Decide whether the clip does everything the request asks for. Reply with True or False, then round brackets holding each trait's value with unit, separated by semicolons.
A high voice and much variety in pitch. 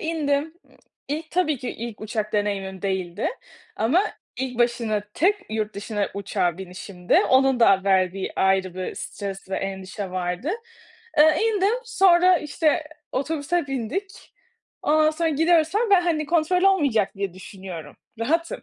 True (245 Hz; 8.9 semitones)